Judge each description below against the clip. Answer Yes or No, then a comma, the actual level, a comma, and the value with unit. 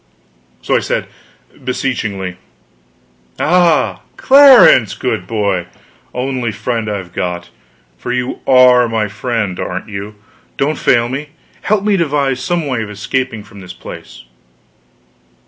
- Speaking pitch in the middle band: No, low, 120 Hz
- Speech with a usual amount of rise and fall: Yes, average, 5.0 semitones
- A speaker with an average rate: No, slow, 130 wpm